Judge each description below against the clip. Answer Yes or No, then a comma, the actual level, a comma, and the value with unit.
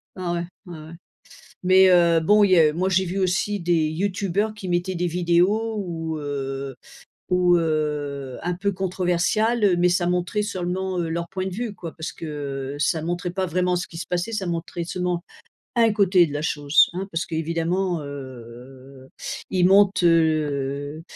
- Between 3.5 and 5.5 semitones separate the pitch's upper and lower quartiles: No, average, 3.1 semitones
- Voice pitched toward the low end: No, medium, 175 Hz